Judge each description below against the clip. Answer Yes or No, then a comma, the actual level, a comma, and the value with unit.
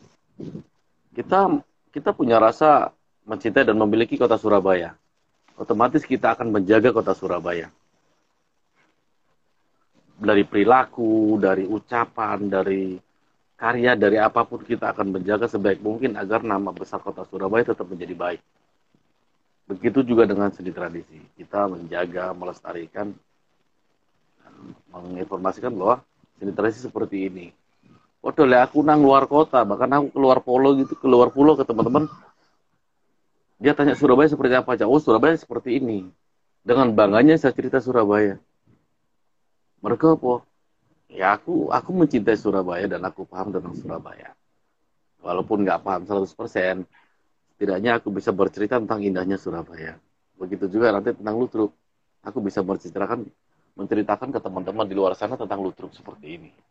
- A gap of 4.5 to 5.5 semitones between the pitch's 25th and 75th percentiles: Yes, average, 5.0 semitones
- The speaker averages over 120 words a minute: Yes, average, 130 wpm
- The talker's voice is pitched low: Yes, low, 105 Hz